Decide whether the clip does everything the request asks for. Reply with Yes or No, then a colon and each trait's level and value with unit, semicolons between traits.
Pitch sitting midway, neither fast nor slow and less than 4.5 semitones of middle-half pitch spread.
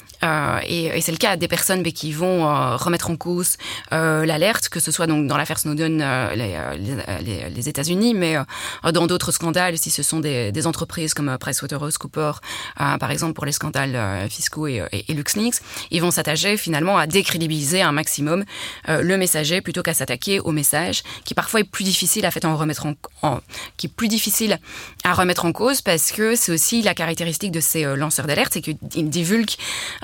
Yes: medium, 160 Hz; average, 205 wpm; average, 3.3 semitones